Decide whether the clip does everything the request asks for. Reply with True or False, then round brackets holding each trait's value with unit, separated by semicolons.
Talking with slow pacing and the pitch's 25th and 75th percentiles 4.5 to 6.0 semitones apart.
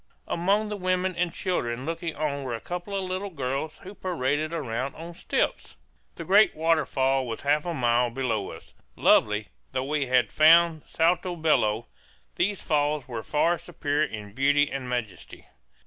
False (165 wpm; 5.2 semitones)